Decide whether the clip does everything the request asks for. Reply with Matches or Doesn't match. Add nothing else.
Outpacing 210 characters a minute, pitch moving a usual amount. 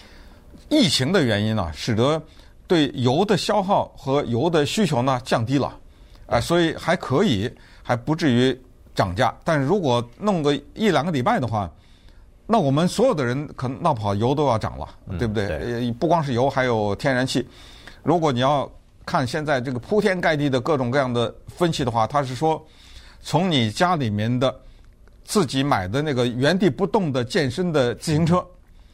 Matches